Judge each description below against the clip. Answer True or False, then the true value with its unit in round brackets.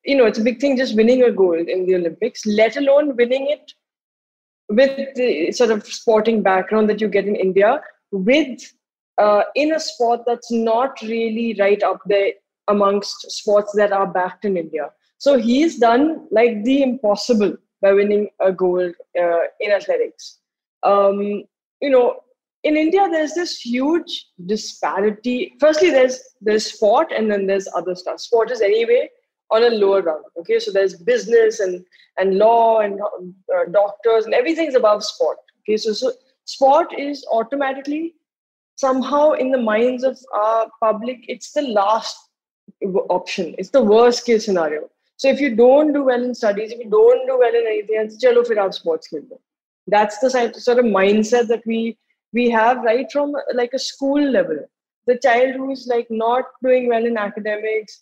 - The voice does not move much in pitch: False (4.4 semitones)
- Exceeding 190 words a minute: False (170 wpm)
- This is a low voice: False (230 Hz)